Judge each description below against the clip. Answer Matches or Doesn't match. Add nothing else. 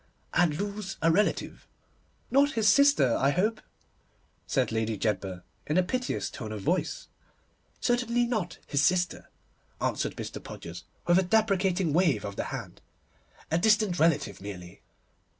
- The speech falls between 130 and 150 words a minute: Matches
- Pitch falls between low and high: Matches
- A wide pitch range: Matches